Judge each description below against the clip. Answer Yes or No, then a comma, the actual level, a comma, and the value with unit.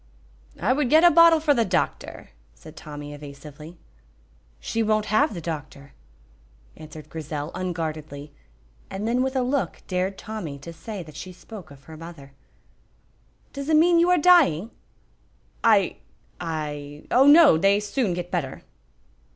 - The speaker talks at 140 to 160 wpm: Yes, average, 150 wpm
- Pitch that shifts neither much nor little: No, wide, 8.5 semitones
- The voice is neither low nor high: Yes, medium, 180 Hz